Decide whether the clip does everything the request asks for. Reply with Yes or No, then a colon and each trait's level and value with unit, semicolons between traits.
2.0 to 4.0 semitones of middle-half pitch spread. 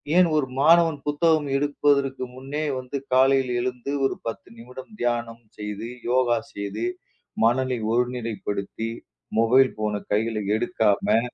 Yes: average, 3.4 semitones